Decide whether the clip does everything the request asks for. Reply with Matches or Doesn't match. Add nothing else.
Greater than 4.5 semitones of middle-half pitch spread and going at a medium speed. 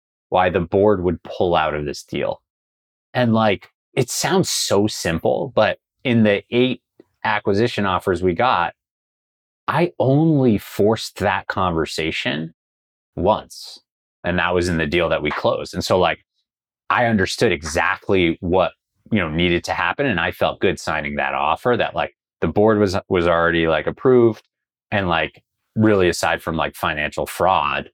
Matches